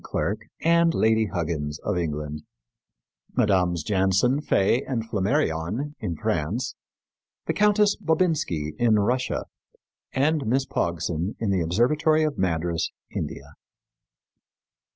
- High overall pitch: No, low, 105 Hz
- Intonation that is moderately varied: No, wide, 8.6 semitones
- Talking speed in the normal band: No, slow, 110 wpm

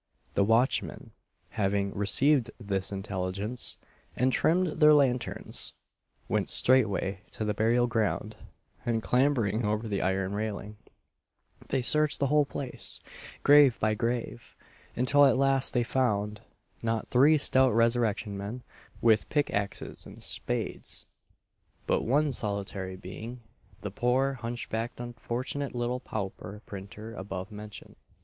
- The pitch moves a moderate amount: Yes, average, 4.0 semitones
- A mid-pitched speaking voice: No, low, 115 Hz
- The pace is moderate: No, slow, 125 wpm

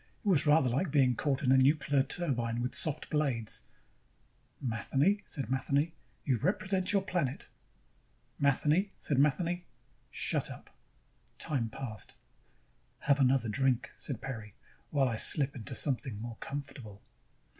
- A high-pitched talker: No, medium, 140 Hz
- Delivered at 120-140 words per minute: Yes, slow, 135 wpm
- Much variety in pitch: No, average, 3.5 semitones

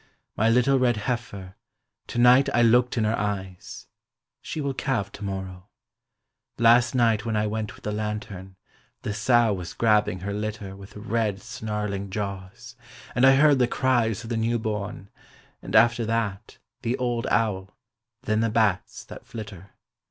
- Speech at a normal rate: Yes, average, 160 wpm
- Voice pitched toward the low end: Yes, low, 110 Hz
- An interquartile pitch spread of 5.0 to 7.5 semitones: No, average, 2.8 semitones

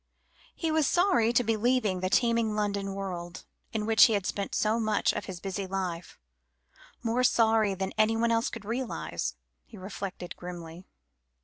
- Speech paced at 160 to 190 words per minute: Yes, average, 165 wpm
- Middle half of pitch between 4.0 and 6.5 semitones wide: No, average, 3.5 semitones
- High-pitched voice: Yes, high, 210 Hz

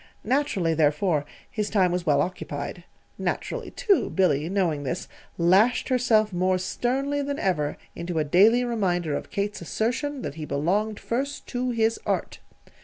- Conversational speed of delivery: Yes, average, 150 wpm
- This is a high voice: Yes, high, 195 Hz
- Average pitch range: No, wide, 6.3 semitones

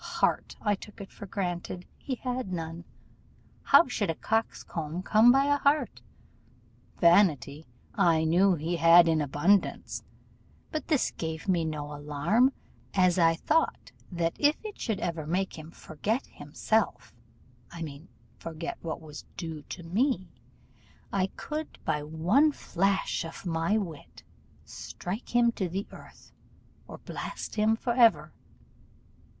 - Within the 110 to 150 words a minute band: Yes, average, 140 wpm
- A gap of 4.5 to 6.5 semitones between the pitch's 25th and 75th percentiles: Yes, average, 5.3 semitones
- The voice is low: No, medium, 175 Hz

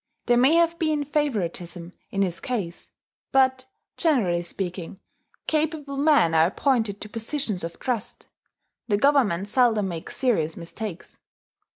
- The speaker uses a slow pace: Yes, slow, 130 wpm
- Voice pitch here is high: Yes, high, 220 Hz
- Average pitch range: No, wide, 7.8 semitones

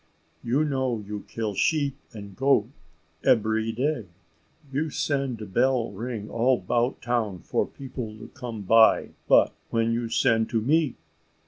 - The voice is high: No, low, 115 Hz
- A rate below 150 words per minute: Yes, average, 140 wpm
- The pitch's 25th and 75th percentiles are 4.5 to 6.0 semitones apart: No, average, 3.1 semitones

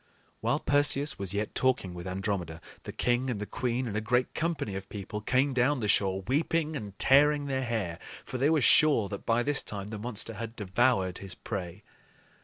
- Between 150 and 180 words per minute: No, average, 200 wpm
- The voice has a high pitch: No, low, 115 Hz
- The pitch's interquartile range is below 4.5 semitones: No, average, 5.1 semitones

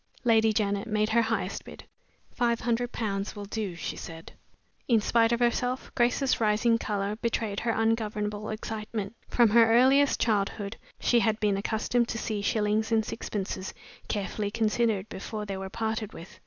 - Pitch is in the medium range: No, high, 220 Hz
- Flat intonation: Yes, narrow, 2.0 semitones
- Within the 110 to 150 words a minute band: No, average, 160 wpm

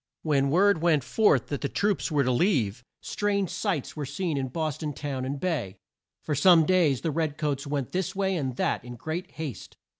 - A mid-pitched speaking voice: Yes, medium, 150 Hz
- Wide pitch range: No, average, 4.5 semitones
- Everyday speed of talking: No, fast, 210 wpm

